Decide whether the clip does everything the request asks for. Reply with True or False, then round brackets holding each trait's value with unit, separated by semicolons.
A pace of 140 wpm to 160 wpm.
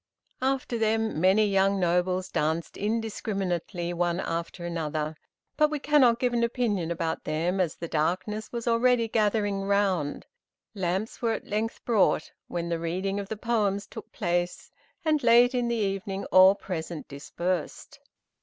True (150 wpm)